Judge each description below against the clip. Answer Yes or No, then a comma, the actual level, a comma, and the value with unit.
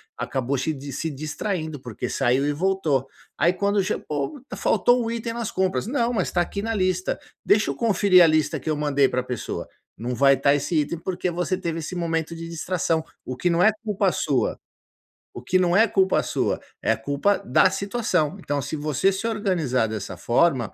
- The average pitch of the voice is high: No, medium, 170 Hz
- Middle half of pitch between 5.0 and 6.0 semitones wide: Yes, average, 5.3 semitones